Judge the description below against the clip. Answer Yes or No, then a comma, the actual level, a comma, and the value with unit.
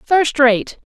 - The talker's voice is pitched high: Yes, very high, 275 Hz